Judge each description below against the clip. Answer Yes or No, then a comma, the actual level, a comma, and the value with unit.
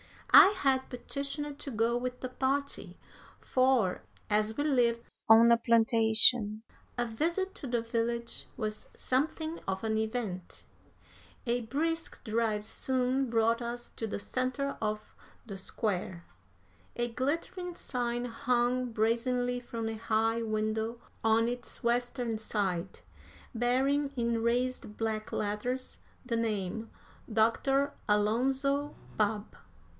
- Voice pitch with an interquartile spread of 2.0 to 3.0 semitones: Yes, narrow, 2.6 semitones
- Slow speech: Yes, slow, 120 wpm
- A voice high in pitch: Yes, high, 235 Hz